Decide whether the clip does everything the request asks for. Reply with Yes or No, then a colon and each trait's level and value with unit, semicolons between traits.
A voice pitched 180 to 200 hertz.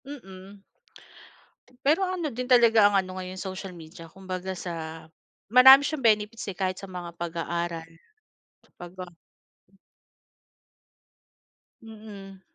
Yes: high, 190 Hz